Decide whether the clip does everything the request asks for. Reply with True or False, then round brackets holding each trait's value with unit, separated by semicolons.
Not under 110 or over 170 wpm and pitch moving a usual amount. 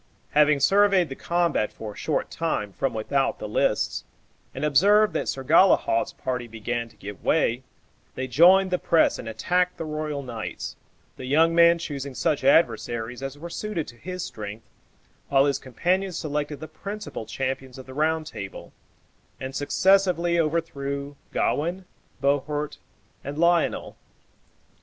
True (145 wpm; 4.7 semitones)